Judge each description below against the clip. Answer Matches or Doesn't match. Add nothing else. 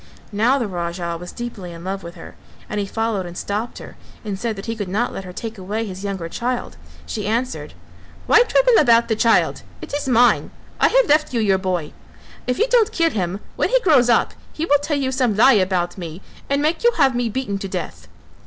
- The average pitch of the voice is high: Matches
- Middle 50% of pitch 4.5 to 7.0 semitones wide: Matches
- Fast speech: Matches